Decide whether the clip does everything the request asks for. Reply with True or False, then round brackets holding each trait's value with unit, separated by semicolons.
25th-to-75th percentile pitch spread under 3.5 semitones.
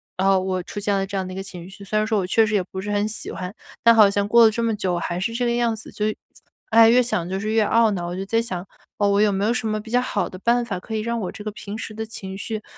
True (2.8 semitones)